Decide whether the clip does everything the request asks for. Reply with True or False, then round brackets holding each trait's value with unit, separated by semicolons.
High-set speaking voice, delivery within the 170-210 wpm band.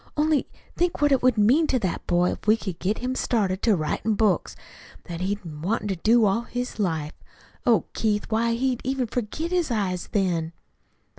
True (215 Hz; 190 wpm)